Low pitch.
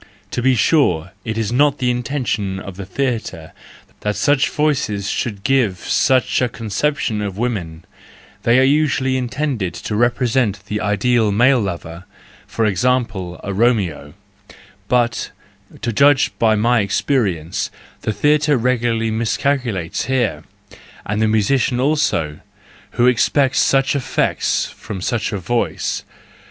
Yes: low, 115 Hz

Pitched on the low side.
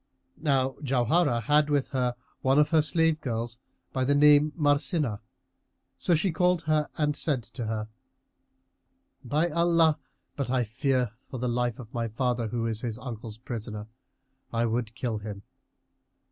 Yes: low, 130 Hz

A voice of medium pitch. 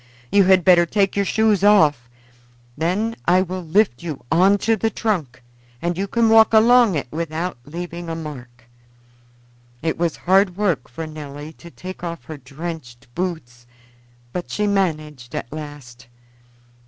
Yes: medium, 170 Hz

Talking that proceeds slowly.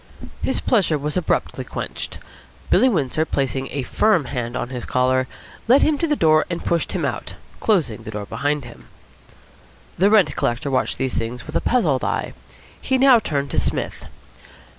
No: average, 175 wpm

